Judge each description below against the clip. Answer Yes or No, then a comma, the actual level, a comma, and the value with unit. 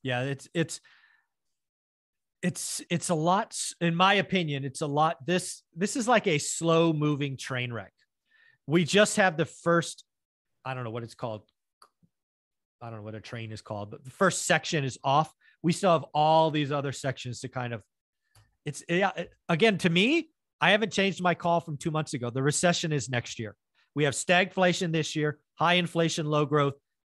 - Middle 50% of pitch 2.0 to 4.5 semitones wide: No, average, 4.9 semitones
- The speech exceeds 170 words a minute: Yes, average, 190 wpm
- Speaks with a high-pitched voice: No, medium, 160 Hz